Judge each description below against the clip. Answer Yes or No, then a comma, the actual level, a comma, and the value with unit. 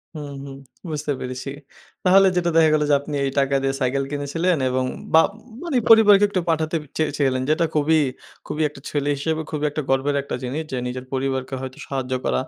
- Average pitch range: Yes, average, 3.1 semitones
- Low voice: No, medium, 145 Hz